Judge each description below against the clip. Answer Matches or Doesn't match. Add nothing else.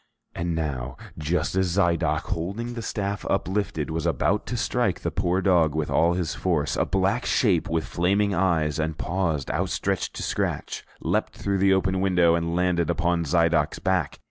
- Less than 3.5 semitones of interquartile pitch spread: Matches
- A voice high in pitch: Doesn't match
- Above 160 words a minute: Matches